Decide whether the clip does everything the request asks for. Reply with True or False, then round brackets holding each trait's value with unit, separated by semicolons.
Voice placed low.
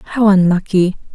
False (190 Hz)